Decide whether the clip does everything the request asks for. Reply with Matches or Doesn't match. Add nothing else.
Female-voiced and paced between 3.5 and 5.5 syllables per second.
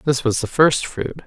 Doesn't match